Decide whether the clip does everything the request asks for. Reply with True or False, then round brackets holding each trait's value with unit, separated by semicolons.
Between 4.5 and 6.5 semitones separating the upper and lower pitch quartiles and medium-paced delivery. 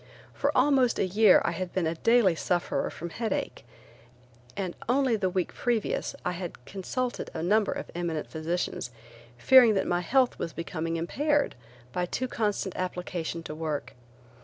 True (5.3 semitones; 160 wpm)